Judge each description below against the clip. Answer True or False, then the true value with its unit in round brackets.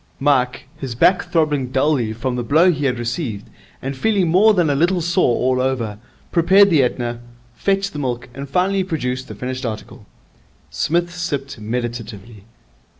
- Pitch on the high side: False (135 Hz)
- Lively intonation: True (6.0 semitones)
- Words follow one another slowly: False (160 wpm)